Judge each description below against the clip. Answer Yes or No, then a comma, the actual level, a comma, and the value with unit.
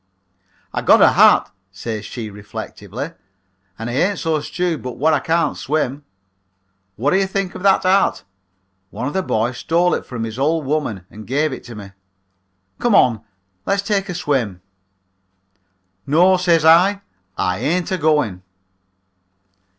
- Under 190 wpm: Yes, average, 155 wpm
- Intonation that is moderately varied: No, wide, 7.6 semitones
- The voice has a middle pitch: Yes, medium, 150 Hz